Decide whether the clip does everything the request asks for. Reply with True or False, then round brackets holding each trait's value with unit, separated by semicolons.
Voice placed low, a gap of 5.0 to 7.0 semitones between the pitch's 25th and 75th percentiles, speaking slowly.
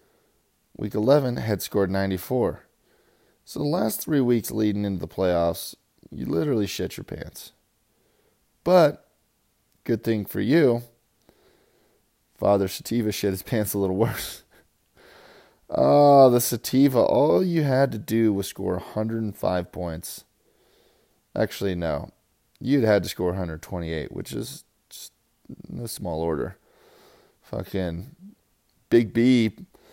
False (105 Hz; 4.0 semitones; 120 wpm)